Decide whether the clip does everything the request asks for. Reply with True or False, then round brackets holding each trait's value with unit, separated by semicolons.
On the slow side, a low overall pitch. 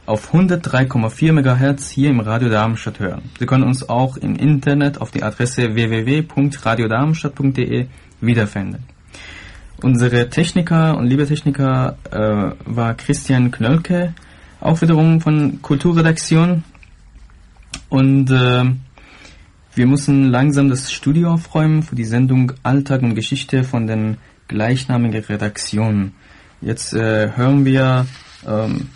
True (110 wpm; 130 Hz)